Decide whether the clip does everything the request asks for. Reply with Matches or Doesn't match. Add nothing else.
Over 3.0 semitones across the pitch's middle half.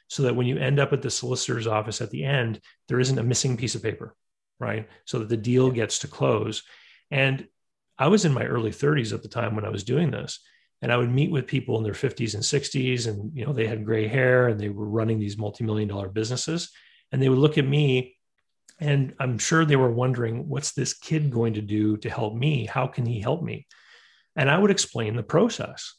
Matches